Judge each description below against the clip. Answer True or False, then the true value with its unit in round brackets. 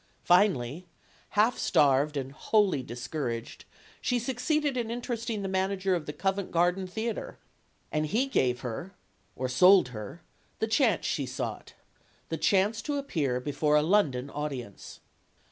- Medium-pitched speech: True (180 Hz)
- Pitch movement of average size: False (7.8 semitones)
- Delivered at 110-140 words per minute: False (150 wpm)